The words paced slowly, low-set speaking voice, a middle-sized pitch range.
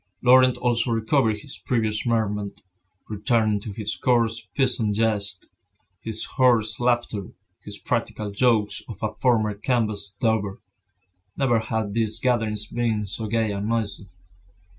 No: slow, 130 wpm; low, 110 Hz; narrow, 2.2 semitones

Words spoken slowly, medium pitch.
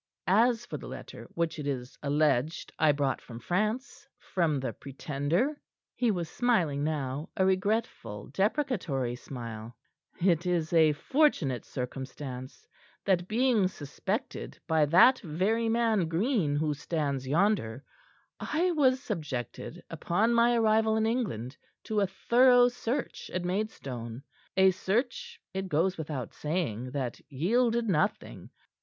Yes: slow, 130 wpm; medium, 175 Hz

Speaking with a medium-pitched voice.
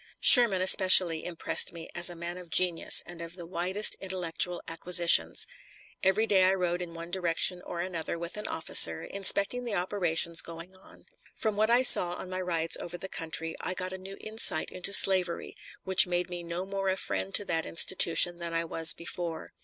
Yes: medium, 180 Hz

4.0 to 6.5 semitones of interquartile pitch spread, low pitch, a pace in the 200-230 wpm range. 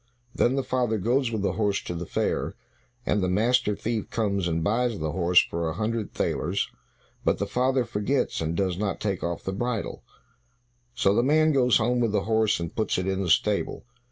Yes: average, 4.5 semitones; low, 105 Hz; fast, 205 wpm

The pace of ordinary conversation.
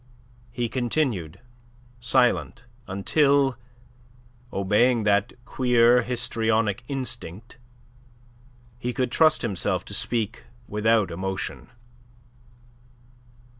No: slow, 75 wpm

